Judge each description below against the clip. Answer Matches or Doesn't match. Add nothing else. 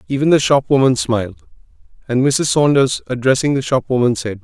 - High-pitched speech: Doesn't match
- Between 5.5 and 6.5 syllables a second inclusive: Matches